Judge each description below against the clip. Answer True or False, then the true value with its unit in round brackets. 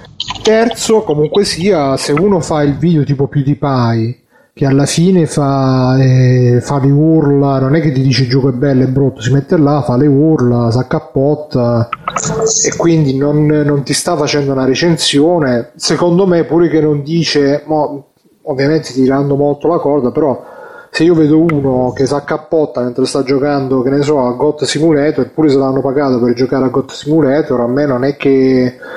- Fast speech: True (180 wpm)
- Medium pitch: True (145 Hz)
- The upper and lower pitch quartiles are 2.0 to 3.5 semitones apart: True (2.8 semitones)